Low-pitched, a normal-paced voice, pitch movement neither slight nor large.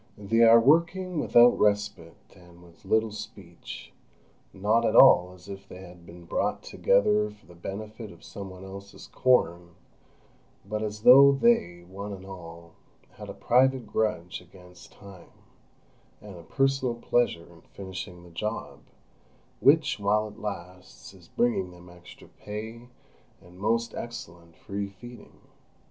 Yes: low, 100 Hz; average, 145 wpm; average, 4.3 semitones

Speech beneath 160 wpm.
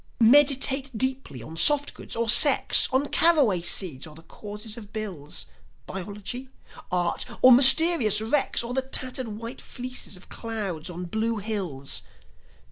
Yes: slow, 135 wpm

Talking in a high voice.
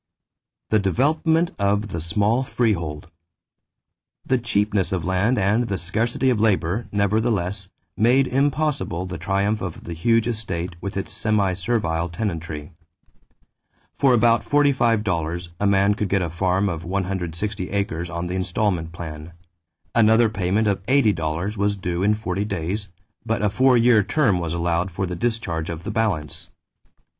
No: low, 100 Hz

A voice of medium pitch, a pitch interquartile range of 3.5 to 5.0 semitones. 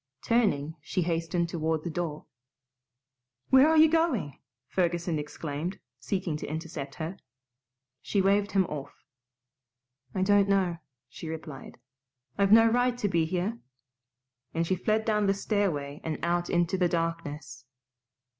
Yes: medium, 175 Hz; average, 4.1 semitones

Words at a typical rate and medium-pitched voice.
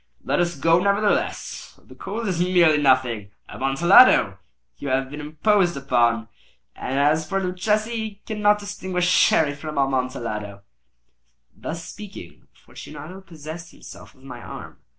No: slow, 130 wpm; medium, 160 Hz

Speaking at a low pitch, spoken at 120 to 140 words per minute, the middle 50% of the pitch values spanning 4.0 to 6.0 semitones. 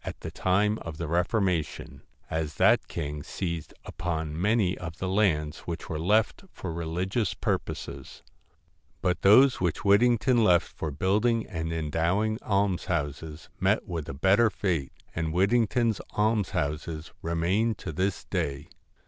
Yes: very low, 90 Hz; slow, 135 wpm; average, 4.5 semitones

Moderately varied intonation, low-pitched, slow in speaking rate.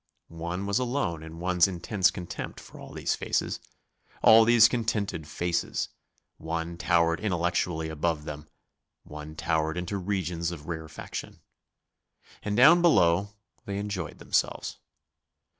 Yes: average, 3.7 semitones; very low, 85 Hz; slow, 125 wpm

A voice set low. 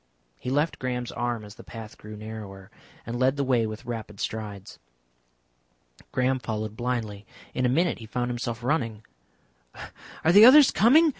Yes: low, 120 Hz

